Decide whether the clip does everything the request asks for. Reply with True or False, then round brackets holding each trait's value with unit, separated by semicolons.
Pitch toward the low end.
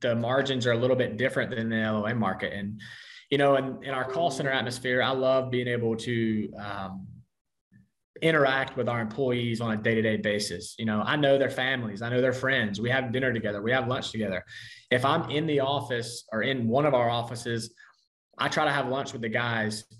True (120 Hz)